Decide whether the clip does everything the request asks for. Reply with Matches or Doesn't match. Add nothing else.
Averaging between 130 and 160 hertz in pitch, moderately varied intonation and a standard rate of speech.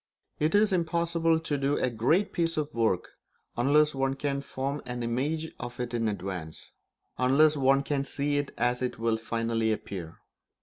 Matches